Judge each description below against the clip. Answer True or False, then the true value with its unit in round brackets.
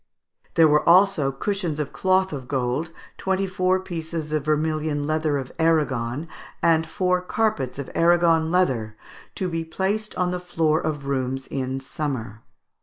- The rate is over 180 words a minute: False (150 wpm)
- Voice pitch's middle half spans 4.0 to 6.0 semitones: True (4.5 semitones)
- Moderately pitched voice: True (160 Hz)